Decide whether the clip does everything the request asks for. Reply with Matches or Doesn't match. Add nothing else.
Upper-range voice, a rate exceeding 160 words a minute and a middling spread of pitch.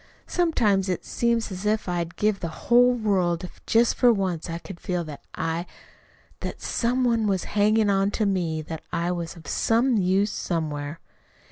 Matches